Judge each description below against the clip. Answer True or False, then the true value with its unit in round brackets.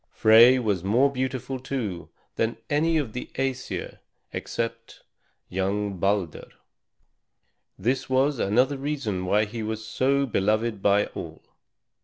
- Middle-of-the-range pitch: False (115 Hz)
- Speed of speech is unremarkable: False (120 wpm)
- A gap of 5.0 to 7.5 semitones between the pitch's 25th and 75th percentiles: False (4.3 semitones)